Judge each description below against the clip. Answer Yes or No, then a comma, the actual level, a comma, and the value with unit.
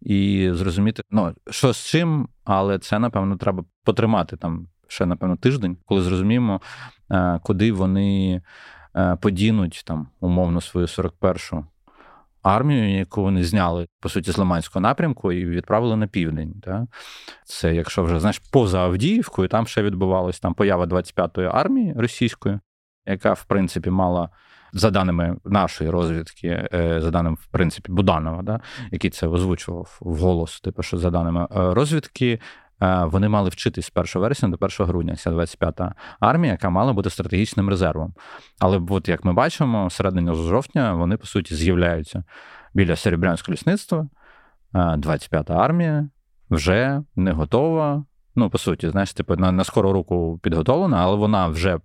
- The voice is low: Yes, very low, 95 Hz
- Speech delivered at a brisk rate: No, average, 140 wpm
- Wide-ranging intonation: No, average, 3.4 semitones